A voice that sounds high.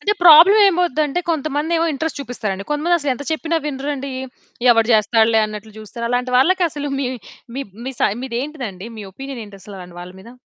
Yes: very high, 270 Hz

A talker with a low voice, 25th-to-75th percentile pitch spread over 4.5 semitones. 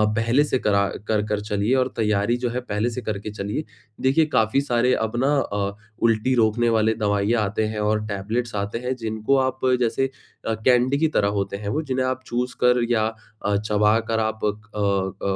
No: low, 110 Hz; average, 2.9 semitones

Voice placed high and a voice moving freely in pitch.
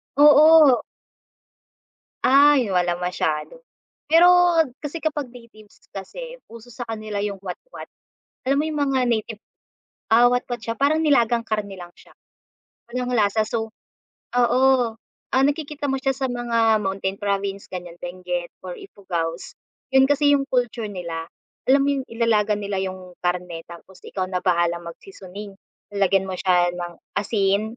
Yes: high, 215 Hz; wide, 5.9 semitones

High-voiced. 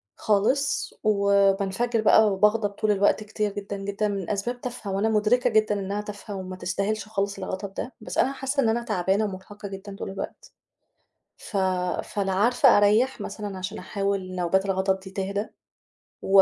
Yes: high, 205 Hz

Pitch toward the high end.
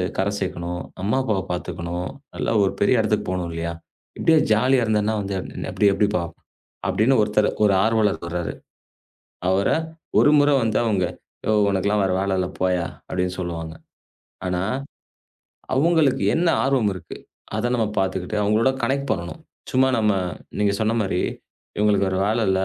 No: low, 105 Hz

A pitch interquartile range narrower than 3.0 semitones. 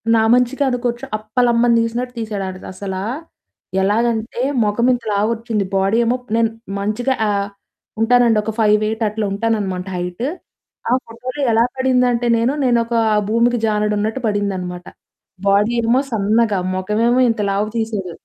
Yes: narrow, 2.6 semitones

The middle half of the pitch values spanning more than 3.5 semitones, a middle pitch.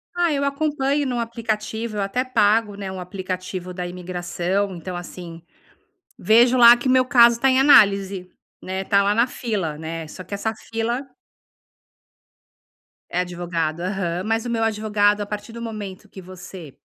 No: average, 4.3 semitones; high, 205 Hz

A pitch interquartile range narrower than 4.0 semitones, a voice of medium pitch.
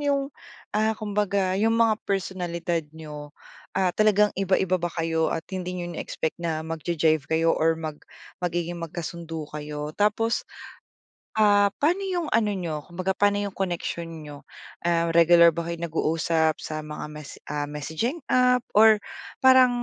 No: average, 4.3 semitones; medium, 175 Hz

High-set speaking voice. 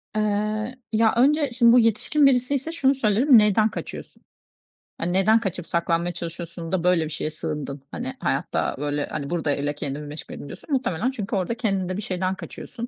Yes: high, 195 Hz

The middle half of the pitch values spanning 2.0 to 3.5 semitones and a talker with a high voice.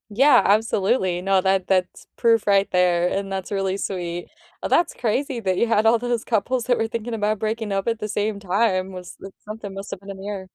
Yes: average, 2.9 semitones; high, 200 Hz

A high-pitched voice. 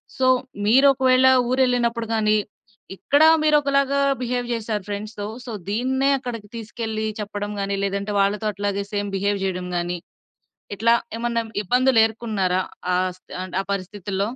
Yes: high, 220 Hz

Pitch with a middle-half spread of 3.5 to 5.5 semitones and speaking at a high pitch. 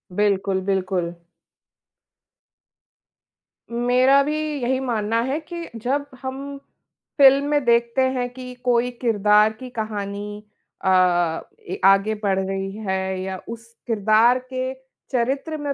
Yes: average, 4.5 semitones; high, 235 Hz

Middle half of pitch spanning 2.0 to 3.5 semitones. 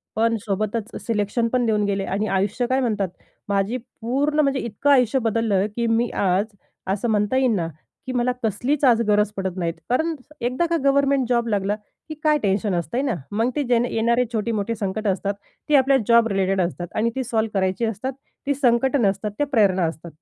No: average, 4.0 semitones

